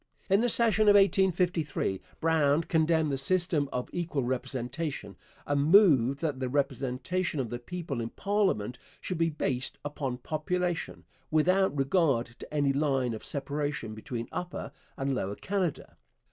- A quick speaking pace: No, average, 145 wpm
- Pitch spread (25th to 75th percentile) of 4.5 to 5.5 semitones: Yes, average, 5.2 semitones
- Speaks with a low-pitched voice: No, medium, 145 Hz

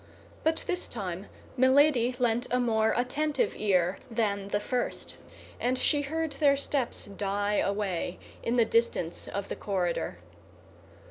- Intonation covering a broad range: No, average, 4.6 semitones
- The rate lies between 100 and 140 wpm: Yes, slow, 135 wpm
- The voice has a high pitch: Yes, high, 230 Hz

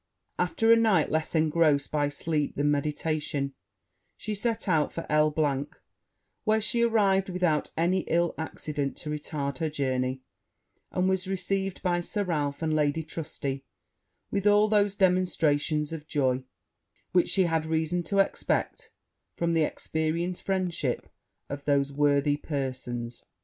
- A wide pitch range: No, average, 4.2 semitones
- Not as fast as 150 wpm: Yes, average, 140 wpm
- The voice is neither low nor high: Yes, medium, 160 Hz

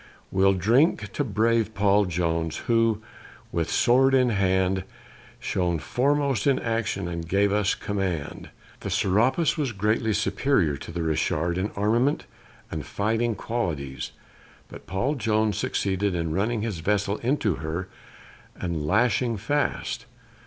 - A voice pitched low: Yes, low, 100 Hz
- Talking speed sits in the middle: No, slow, 130 wpm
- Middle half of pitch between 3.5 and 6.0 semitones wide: Yes, average, 4.6 semitones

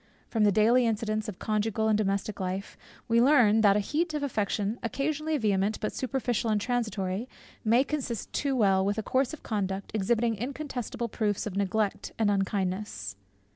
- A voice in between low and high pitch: No, high, 215 Hz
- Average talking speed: Yes, average, 170 wpm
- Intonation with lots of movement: No, average, 3.3 semitones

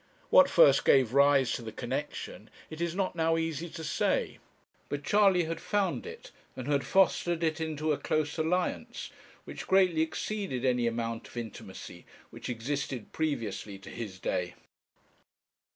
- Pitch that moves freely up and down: Yes, wide, 6.0 semitones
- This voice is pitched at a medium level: Yes, medium, 155 Hz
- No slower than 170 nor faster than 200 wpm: No, average, 150 wpm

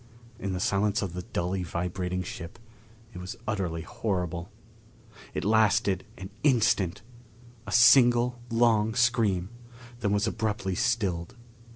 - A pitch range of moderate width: Yes, average, 4.0 semitones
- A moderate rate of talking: No, slow, 120 wpm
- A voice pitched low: Yes, low, 100 Hz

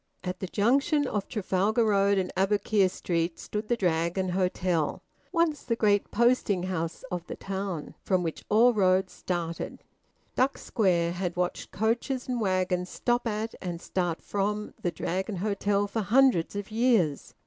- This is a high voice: Yes, high, 195 Hz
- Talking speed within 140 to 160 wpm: Yes, average, 155 wpm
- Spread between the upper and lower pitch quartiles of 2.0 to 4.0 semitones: Yes, average, 3.5 semitones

